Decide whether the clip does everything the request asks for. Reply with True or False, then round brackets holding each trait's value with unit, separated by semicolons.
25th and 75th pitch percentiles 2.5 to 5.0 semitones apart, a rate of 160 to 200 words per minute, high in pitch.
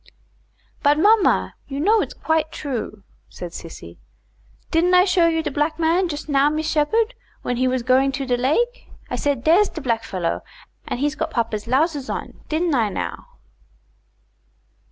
True (4.5 semitones; 165 wpm; 295 Hz)